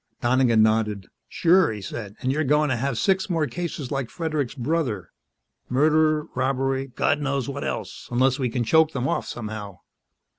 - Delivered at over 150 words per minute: Yes, average, 170 wpm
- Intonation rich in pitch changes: No, average, 4.3 semitones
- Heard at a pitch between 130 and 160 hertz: Yes, low, 135 Hz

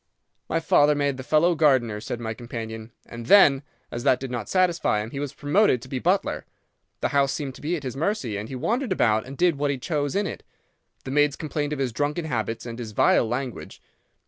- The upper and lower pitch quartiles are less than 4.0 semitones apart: No, average, 4.3 semitones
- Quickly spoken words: Yes, fast, 225 wpm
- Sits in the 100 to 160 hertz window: Yes, low, 135 Hz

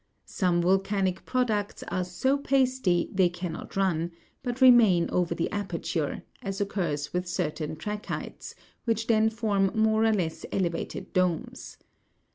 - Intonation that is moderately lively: Yes, average, 4.0 semitones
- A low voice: No, high, 195 Hz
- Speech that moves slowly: Yes, slow, 130 wpm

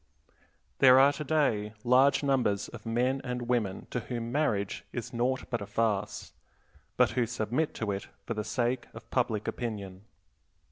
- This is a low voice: Yes, low, 120 Hz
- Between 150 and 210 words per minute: Yes, average, 155 wpm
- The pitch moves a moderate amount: Yes, average, 3.4 semitones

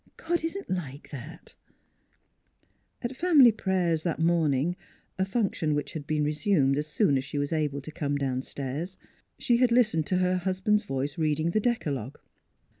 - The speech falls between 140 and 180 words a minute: Yes, average, 170 wpm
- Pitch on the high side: No, medium, 165 Hz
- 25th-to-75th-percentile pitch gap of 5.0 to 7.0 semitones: Yes, wide, 5.6 semitones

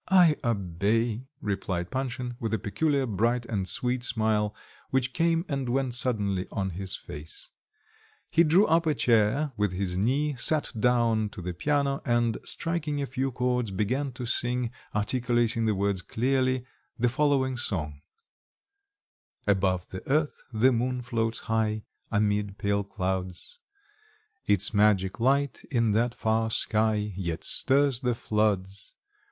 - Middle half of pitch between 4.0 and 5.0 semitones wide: Yes, average, 4.3 semitones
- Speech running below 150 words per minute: Yes, average, 140 wpm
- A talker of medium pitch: No, low, 115 Hz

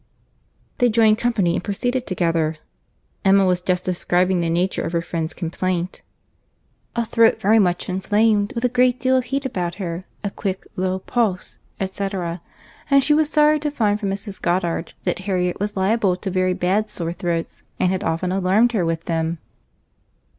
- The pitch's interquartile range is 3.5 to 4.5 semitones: Yes, average, 4.0 semitones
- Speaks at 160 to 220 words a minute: Yes, average, 170 wpm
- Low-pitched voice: No, high, 190 Hz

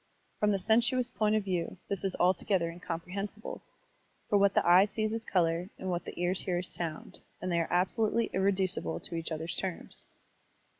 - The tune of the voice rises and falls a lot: No, average, 3.1 semitones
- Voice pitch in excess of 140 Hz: Yes, medium, 185 Hz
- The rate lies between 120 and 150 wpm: No, average, 185 wpm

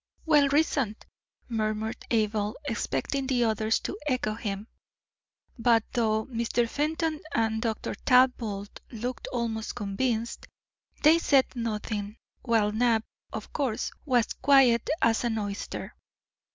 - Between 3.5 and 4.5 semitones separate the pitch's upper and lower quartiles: No, average, 3.1 semitones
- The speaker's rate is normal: No, slow, 115 wpm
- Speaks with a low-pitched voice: No, high, 230 Hz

